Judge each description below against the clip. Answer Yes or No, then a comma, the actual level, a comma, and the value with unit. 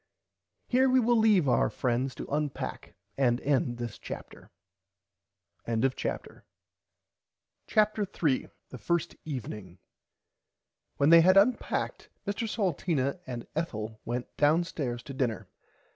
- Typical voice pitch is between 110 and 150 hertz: Yes, medium, 140 Hz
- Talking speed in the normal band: No, slow, 115 wpm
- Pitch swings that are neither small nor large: No, wide, 7.5 semitones